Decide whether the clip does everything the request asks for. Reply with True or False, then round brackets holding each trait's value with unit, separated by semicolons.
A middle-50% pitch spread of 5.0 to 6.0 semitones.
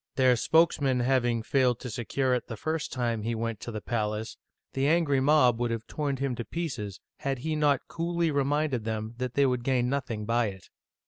False (3.5 semitones)